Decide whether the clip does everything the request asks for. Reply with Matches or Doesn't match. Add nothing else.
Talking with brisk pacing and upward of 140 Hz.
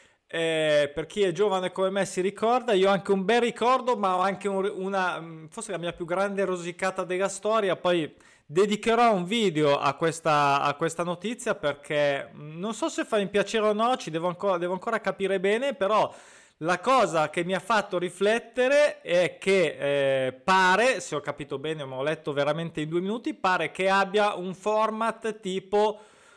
Matches